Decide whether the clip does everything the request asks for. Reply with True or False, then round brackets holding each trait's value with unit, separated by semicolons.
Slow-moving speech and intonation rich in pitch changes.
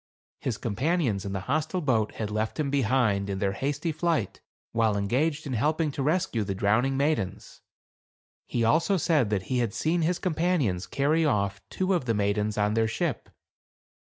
False (180 wpm; 7.1 semitones)